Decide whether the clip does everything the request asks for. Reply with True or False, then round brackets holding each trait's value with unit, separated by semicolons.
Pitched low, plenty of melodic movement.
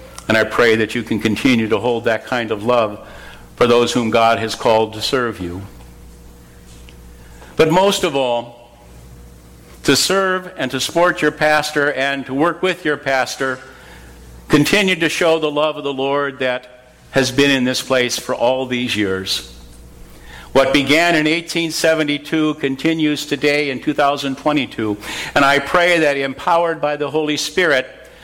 True (130 Hz; 5.9 semitones)